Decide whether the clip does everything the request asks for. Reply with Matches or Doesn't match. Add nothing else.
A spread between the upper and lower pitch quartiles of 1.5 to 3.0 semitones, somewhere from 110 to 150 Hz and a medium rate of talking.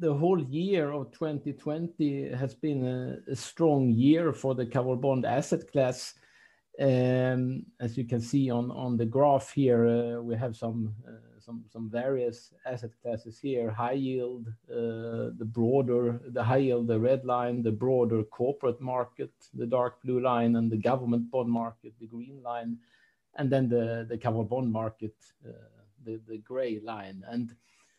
Matches